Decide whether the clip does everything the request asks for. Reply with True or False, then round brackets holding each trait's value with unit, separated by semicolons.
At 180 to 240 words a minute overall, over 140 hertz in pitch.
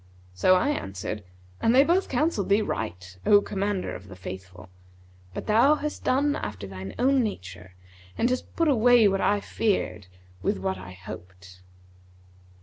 False (155 wpm; 185 Hz)